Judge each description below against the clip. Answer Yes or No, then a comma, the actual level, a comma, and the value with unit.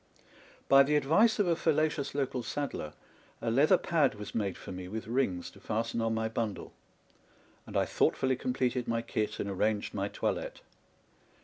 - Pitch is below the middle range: Yes, low, 120 Hz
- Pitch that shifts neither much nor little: Yes, average, 4.9 semitones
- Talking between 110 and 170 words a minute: No, average, 180 wpm